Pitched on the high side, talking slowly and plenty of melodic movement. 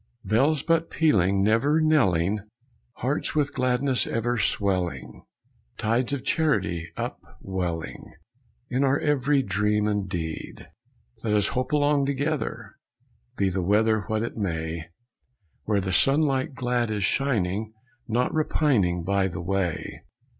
No: low, 110 Hz; slow, 125 wpm; wide, 6.2 semitones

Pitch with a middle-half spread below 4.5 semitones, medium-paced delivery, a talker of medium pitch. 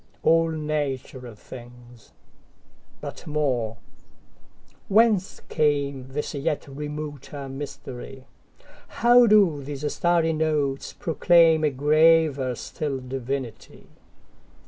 No: average, 3.1 semitones; slow, 70 wpm; medium, 145 Hz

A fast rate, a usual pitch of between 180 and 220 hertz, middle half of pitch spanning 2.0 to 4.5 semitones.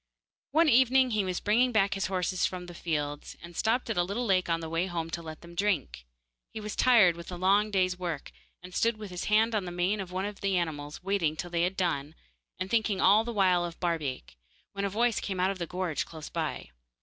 Yes: fast, 240 wpm; medium, 185 Hz; average, 3.4 semitones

